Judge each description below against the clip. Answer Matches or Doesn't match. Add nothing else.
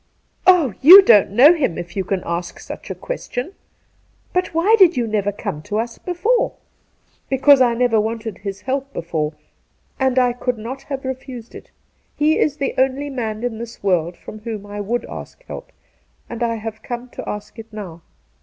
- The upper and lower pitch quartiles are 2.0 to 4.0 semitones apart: Doesn't match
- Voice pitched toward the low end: Doesn't match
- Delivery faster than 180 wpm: Matches